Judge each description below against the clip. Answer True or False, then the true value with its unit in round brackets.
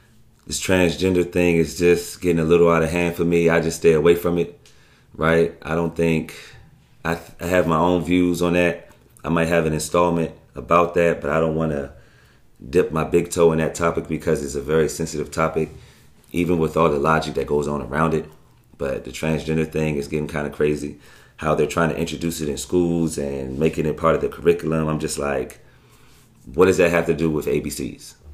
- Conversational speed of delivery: False (215 wpm)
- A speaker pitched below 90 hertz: True (80 Hz)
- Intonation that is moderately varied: False (1.8 semitones)